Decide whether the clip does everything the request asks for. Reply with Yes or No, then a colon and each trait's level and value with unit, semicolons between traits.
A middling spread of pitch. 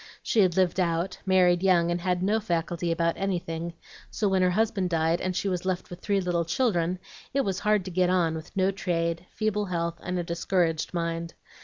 No: narrow, 2.1 semitones